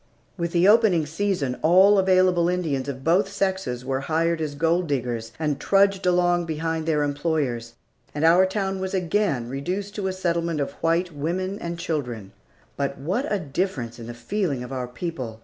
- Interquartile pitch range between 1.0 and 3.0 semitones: No, average, 5.2 semitones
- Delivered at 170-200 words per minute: Yes, average, 175 wpm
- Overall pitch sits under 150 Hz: No, medium, 165 Hz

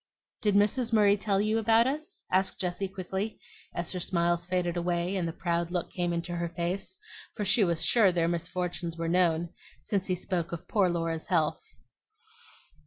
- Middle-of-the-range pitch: Yes, medium, 180 Hz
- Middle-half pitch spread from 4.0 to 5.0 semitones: No, average, 2.8 semitones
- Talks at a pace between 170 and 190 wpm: Yes, average, 175 wpm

